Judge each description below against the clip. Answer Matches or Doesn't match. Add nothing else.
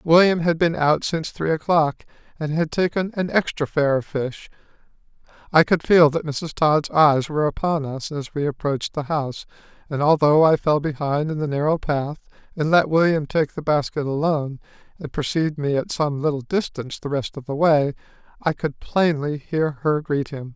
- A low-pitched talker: Doesn't match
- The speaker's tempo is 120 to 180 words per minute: Doesn't match